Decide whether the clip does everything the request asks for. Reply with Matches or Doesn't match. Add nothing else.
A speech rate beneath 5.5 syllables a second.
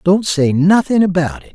Matches